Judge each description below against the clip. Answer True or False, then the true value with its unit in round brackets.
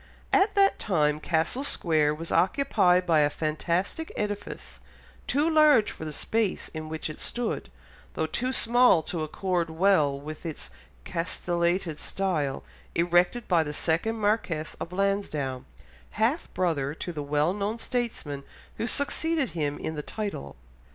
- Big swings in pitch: True (5.9 semitones)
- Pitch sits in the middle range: True (175 Hz)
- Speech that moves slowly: False (145 wpm)